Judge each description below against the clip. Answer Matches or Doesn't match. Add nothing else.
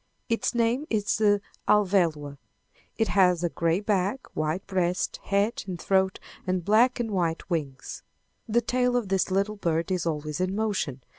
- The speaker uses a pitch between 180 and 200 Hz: Matches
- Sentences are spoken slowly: Doesn't match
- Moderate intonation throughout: Matches